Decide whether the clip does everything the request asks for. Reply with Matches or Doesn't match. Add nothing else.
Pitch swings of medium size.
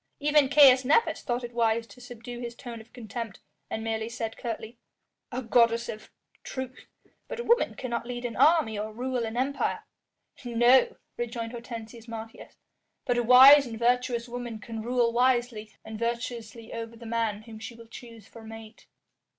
Doesn't match